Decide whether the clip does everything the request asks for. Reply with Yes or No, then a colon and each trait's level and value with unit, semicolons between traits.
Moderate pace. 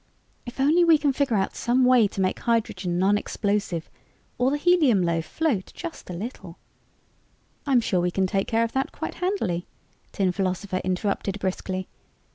Yes: average, 175 wpm